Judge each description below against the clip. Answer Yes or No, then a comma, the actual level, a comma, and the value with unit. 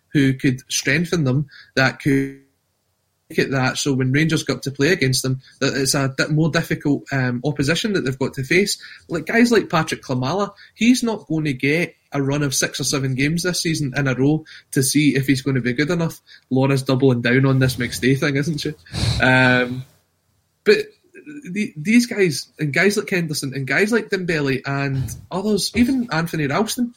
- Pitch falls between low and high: Yes, medium, 145 Hz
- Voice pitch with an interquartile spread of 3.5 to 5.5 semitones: Yes, average, 4.6 semitones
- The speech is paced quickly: No, average, 195 wpm